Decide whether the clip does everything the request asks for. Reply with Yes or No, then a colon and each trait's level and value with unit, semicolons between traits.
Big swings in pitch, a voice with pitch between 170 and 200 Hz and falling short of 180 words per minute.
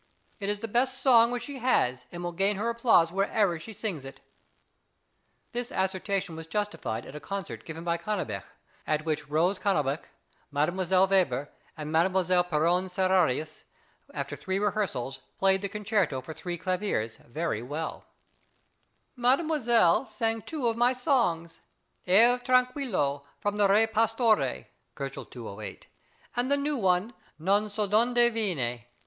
Yes: wide, 5.7 semitones; high, 190 Hz; average, 145 wpm